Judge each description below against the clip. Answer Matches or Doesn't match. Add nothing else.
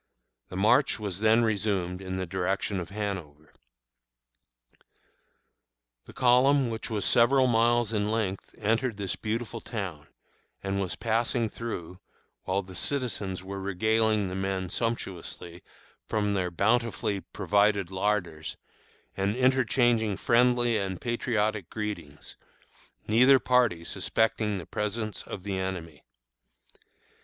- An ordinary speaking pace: Doesn't match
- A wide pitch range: Doesn't match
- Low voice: Matches